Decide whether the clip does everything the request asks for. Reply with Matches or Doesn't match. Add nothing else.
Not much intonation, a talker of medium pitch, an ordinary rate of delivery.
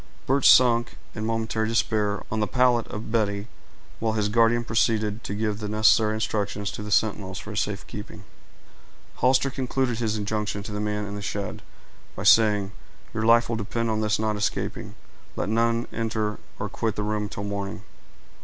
Doesn't match